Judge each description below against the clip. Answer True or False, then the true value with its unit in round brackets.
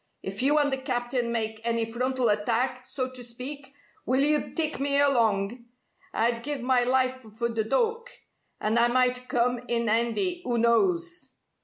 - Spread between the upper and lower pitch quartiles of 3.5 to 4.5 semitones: False (2.9 semitones)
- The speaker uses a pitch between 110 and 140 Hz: False (250 Hz)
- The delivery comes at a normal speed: True (165 wpm)